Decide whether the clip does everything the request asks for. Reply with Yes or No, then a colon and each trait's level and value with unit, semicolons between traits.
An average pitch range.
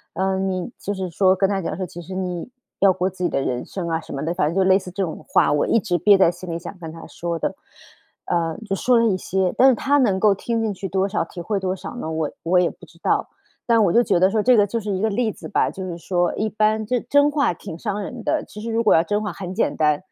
Yes: average, 3.4 semitones